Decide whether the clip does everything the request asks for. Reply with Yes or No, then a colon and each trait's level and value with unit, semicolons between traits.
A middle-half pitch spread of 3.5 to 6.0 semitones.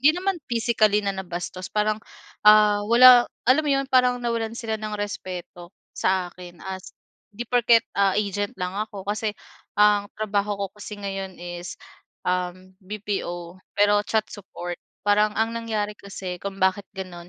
No: average, 2.8 semitones